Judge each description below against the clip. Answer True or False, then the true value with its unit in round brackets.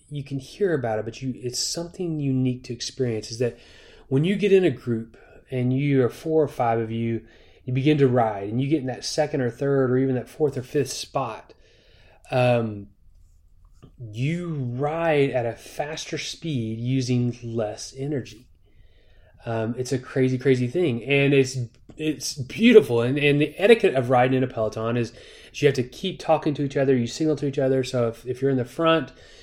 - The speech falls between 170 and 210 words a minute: True (200 wpm)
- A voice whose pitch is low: True (130 Hz)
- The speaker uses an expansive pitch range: False (3.7 semitones)